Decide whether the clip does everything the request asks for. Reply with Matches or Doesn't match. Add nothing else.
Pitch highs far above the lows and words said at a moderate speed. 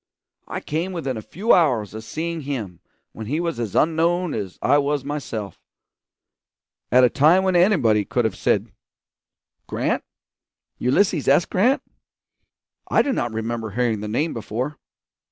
Matches